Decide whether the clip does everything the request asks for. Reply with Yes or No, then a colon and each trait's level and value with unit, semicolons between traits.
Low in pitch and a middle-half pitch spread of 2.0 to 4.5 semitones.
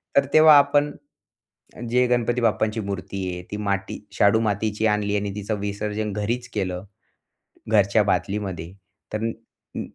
Yes: low, 105 Hz; narrow, 2.4 semitones